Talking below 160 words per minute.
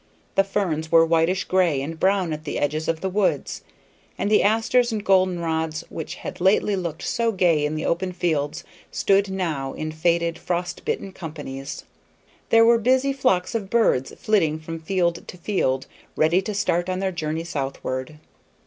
No: average, 175 wpm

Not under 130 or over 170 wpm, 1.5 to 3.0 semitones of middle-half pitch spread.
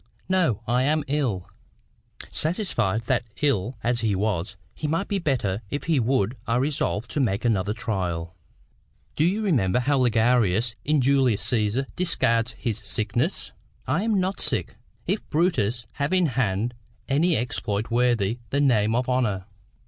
No: average, 150 wpm; average, 5.3 semitones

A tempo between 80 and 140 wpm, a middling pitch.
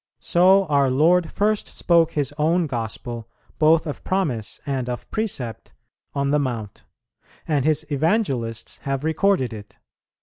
Yes: slow, 135 wpm; medium, 145 Hz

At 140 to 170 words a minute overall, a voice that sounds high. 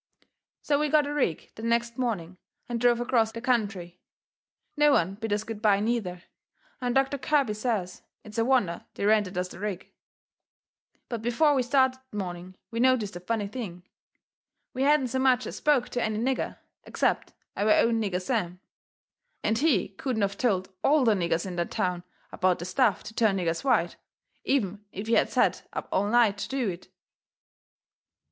No: average, 180 wpm; high, 225 Hz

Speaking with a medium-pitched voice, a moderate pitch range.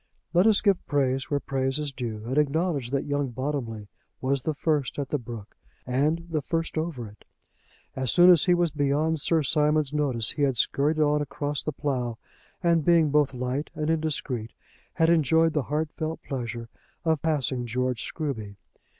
Yes: medium, 145 Hz; average, 3.5 semitones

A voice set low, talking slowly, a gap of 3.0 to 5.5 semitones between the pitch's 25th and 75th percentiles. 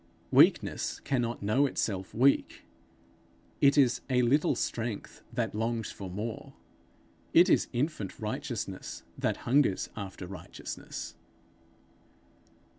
Yes: low, 115 Hz; slow, 105 wpm; average, 4.8 semitones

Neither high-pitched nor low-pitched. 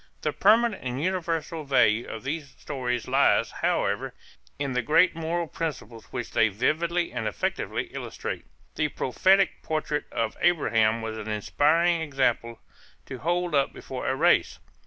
Yes: medium, 145 Hz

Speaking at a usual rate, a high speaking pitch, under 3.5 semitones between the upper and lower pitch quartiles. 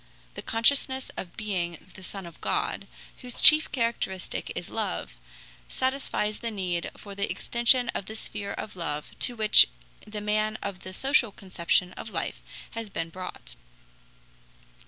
No: average, 150 wpm; high, 210 Hz; average, 4.0 semitones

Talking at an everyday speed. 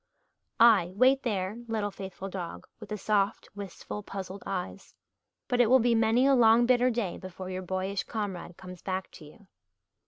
Yes: average, 175 wpm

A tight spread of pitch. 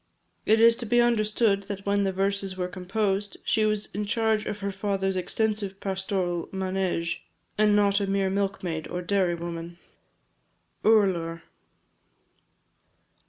Yes: narrow, 2.0 semitones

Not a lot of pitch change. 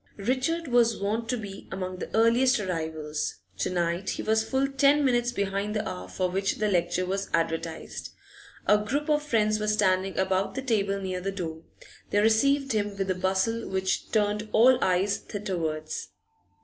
No: average, 3.7 semitones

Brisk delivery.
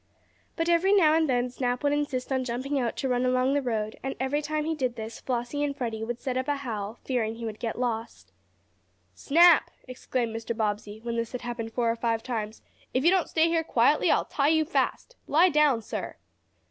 Yes: fast, 215 wpm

